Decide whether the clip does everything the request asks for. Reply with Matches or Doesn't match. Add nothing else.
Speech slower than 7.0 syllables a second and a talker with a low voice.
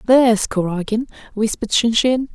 Doesn't match